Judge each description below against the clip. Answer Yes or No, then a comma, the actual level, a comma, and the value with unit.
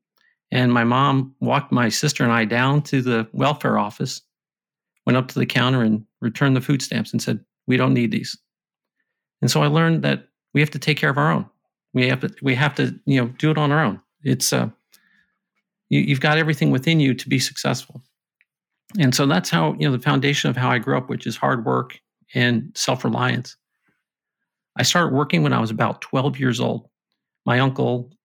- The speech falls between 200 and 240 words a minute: Yes, fast, 205 wpm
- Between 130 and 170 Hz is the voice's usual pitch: Yes, low, 135 Hz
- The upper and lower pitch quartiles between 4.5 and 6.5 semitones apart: No, average, 3.3 semitones